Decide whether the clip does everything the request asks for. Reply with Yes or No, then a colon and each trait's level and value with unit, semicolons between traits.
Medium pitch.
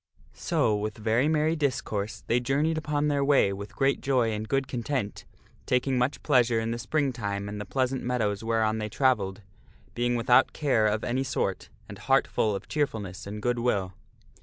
No: low, 120 Hz